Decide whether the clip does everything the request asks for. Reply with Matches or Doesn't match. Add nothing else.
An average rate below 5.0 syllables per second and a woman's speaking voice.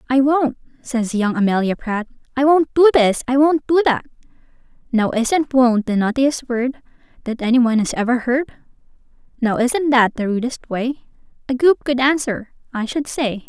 Matches